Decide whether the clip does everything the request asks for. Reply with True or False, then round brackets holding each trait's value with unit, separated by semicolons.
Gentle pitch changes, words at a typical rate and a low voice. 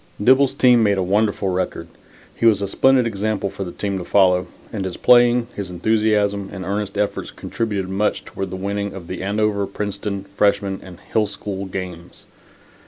True (1.8 semitones; 175 wpm; 100 Hz)